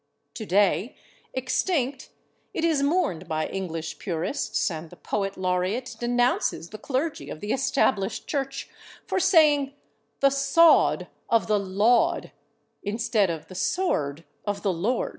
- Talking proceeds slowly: Yes, slow, 130 wpm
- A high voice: Yes, high, 225 Hz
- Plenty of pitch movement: Yes, wide, 6.7 semitones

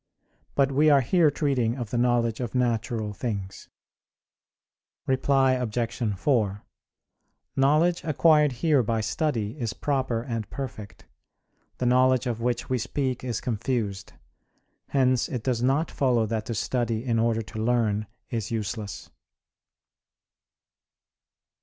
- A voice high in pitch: No, low, 120 Hz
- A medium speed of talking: No, slow, 125 wpm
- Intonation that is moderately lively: Yes, average, 3.0 semitones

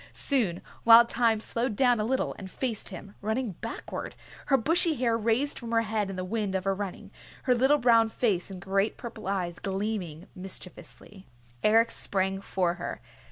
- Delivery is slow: No, average, 175 wpm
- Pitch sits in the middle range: No, high, 215 Hz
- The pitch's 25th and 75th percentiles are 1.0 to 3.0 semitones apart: No, average, 3.6 semitones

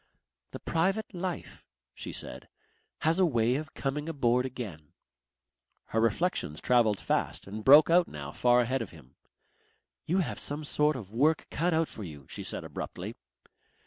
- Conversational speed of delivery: Yes, average, 160 wpm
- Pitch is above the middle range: No, low, 130 Hz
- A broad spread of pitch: Yes, wide, 6.6 semitones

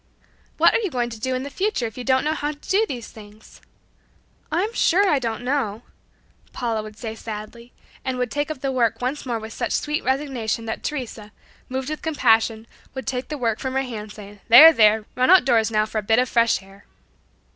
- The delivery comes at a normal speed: No, fast, 215 wpm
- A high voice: Yes, high, 245 Hz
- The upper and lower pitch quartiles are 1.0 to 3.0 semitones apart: No, average, 3.9 semitones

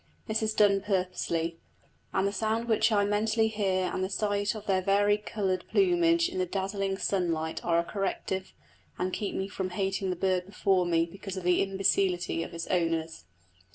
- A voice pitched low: No, high, 195 Hz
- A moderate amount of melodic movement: No, narrow, 2.3 semitones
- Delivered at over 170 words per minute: Yes, average, 185 wpm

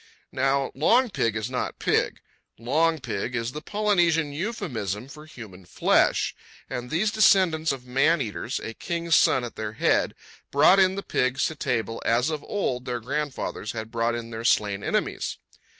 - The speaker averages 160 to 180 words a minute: Yes, average, 165 wpm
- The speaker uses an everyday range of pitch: No, wide, 5.8 semitones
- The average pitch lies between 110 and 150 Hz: Yes, low, 135 Hz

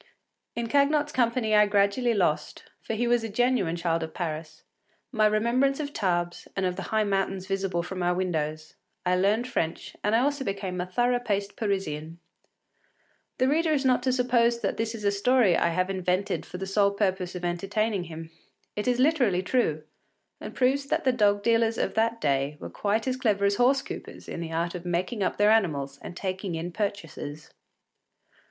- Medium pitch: No, high, 200 Hz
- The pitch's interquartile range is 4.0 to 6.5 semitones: Yes, average, 5.0 semitones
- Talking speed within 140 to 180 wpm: No, average, 190 wpm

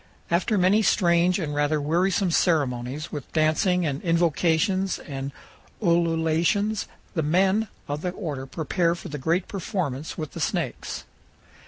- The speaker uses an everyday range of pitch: Yes, average, 3.5 semitones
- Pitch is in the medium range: Yes, medium, 170 Hz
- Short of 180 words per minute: Yes, slow, 135 wpm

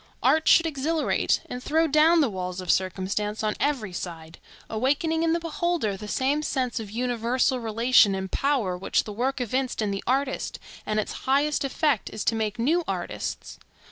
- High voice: Yes, very high, 250 Hz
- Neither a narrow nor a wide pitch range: No, wide, 5.8 semitones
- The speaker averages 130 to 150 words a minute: No, average, 175 wpm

